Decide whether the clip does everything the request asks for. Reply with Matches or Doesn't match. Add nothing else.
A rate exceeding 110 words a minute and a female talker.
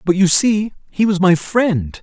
Doesn't match